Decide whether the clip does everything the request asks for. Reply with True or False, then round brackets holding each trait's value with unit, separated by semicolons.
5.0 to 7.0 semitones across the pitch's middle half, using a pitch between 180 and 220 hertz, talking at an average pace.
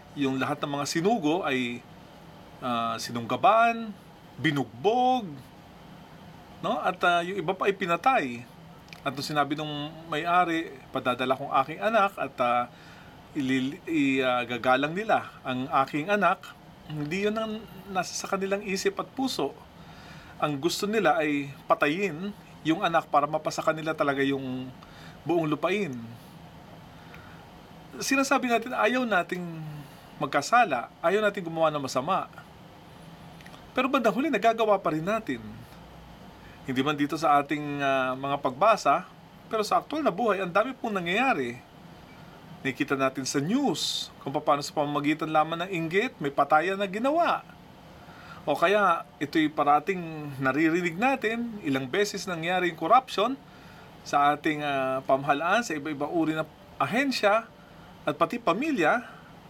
False (5.6 semitones; 165 Hz; 130 wpm)